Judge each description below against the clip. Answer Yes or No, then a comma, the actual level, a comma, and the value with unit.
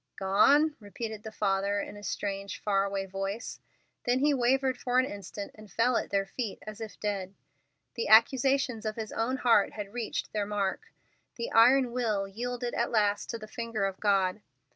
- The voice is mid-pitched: No, high, 215 Hz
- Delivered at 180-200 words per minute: Yes, average, 185 wpm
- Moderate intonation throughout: Yes, average, 3.5 semitones